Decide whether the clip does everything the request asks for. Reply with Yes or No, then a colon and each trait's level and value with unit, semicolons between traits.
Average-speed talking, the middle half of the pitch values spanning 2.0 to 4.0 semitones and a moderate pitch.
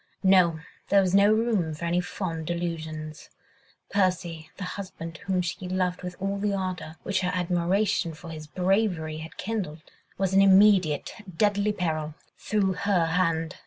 Yes: average, 155 wpm; average, 3.1 semitones; medium, 180 Hz